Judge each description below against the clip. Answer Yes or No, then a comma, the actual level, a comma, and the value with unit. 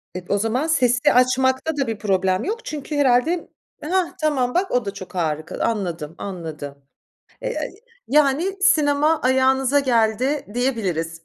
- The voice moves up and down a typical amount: No, wide, 6.9 semitones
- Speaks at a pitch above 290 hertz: No, very high, 255 Hz